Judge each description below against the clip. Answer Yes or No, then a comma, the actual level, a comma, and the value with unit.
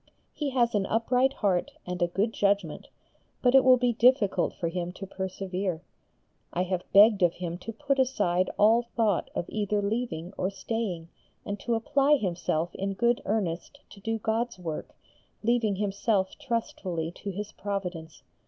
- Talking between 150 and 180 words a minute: Yes, average, 160 wpm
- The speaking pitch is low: No, high, 205 Hz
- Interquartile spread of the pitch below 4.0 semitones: No, average, 4.3 semitones